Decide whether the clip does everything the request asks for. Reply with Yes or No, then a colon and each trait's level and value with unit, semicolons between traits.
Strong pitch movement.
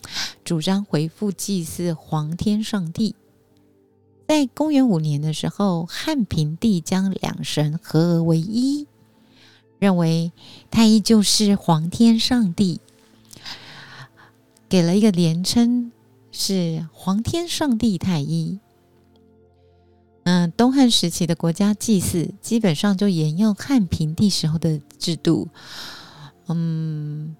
No: average, 4.8 semitones